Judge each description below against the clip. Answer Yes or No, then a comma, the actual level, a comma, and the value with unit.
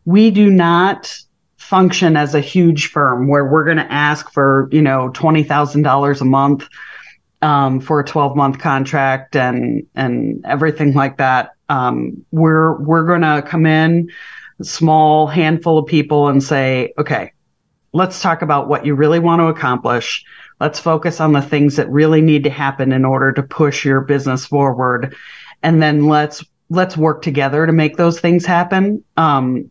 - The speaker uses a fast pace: No, average, 170 wpm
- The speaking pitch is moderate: Yes, medium, 150 Hz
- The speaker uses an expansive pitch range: No, average, 2.8 semitones